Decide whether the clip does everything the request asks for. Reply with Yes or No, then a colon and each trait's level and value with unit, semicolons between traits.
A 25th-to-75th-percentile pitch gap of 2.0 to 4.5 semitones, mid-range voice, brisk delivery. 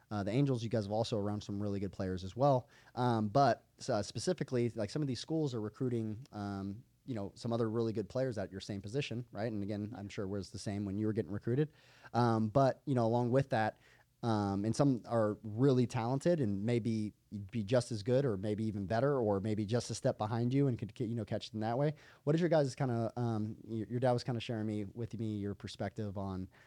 No: average, 3.2 semitones; low, 115 Hz; fast, 245 wpm